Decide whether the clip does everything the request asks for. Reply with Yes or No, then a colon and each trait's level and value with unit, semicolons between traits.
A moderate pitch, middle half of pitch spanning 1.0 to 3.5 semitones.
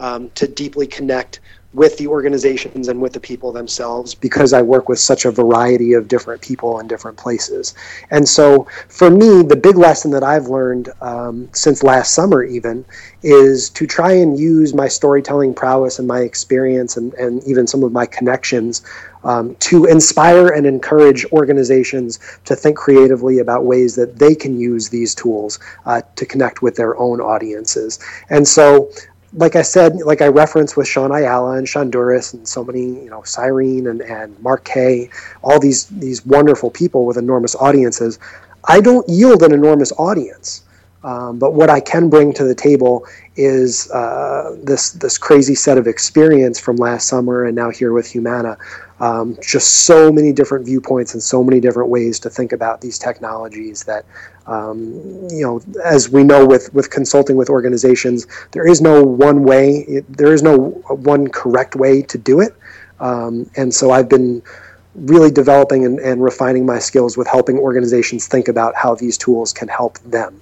No: low, 130 Hz; average, 2.8 semitones